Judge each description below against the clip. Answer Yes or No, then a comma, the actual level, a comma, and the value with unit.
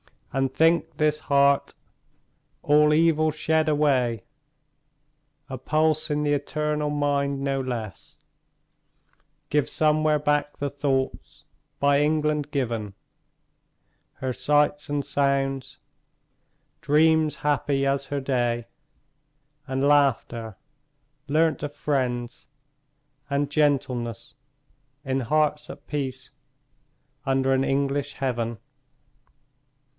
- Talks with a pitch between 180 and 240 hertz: No, medium, 140 Hz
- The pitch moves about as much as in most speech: No, narrow, 2.0 semitones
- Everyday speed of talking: No, slow, 95 wpm